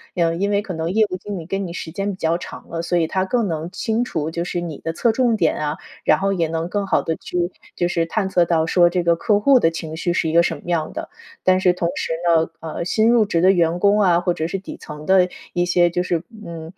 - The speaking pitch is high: No, medium, 175 Hz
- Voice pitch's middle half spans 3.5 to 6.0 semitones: No, average, 2.8 semitones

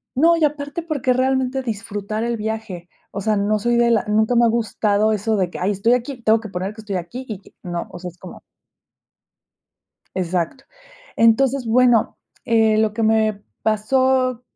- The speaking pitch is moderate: No, high, 220 Hz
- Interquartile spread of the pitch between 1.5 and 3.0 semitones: No, average, 3.4 semitones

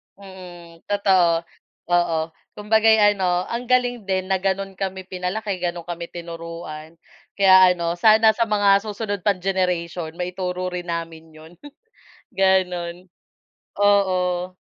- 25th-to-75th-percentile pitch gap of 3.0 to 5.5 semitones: No, narrow, 2.4 semitones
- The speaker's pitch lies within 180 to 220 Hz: Yes, medium, 185 Hz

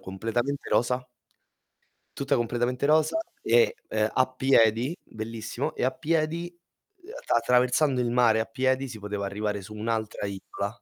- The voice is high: No, low, 125 Hz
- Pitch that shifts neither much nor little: Yes, average, 4.4 semitones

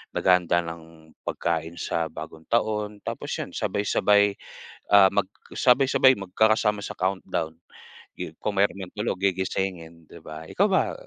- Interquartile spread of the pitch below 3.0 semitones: No, average, 3.9 semitones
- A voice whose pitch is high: No, very low, 95 Hz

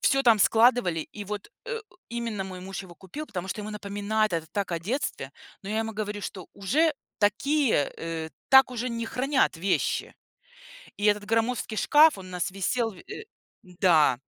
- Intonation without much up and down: No, average, 4.2 semitones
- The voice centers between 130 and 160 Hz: No, high, 210 Hz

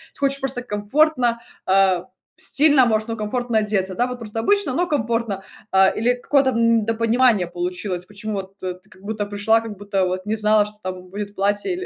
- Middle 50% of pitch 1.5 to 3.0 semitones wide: No, average, 3.9 semitones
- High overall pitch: Yes, high, 215 Hz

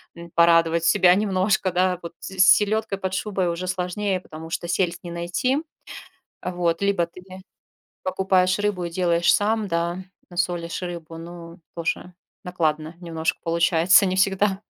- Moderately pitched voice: Yes, medium, 180 Hz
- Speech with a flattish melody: Yes, narrow, 2.0 semitones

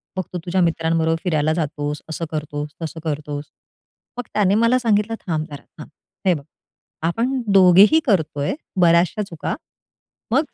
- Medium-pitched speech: Yes, medium, 170 Hz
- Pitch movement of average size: Yes, average, 4.9 semitones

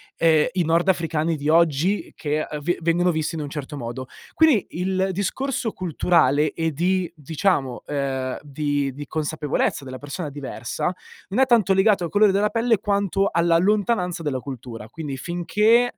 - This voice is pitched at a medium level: Yes, medium, 165 Hz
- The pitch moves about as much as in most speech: Yes, average, 4.8 semitones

